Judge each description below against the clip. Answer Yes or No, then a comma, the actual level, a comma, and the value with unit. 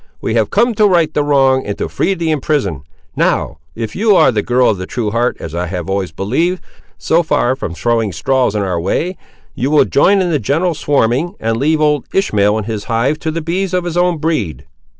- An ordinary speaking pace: No, fast, 225 wpm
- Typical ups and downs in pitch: No, wide, 7.8 semitones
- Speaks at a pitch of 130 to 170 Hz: Yes, low, 135 Hz